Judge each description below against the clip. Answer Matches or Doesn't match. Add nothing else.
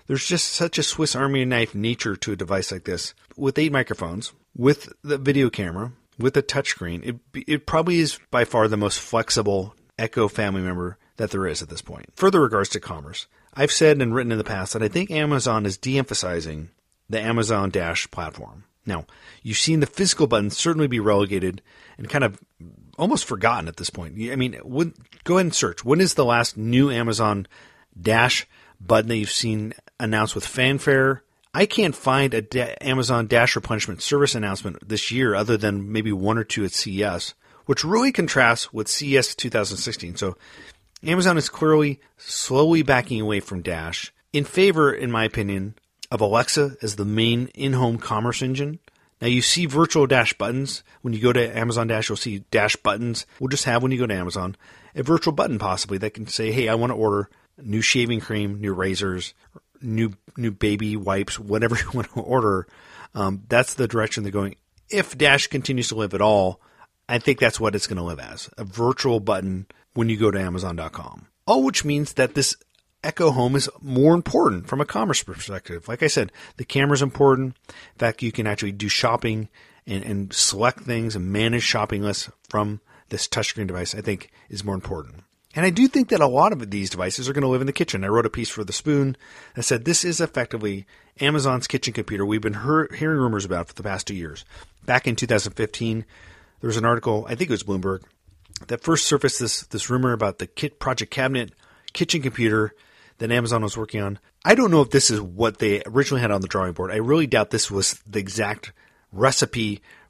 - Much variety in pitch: Doesn't match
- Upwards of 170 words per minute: Matches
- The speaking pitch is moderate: Doesn't match